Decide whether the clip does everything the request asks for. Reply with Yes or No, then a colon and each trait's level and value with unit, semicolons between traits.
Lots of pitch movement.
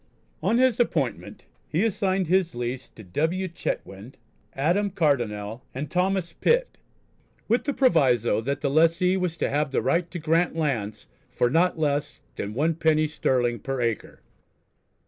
Yes: wide, 6.1 semitones